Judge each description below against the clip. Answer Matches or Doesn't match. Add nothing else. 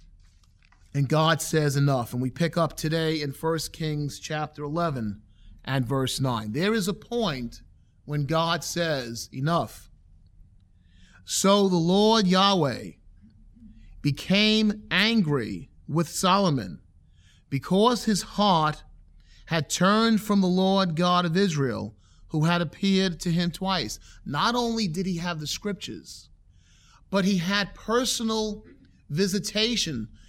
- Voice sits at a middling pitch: Matches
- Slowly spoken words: Matches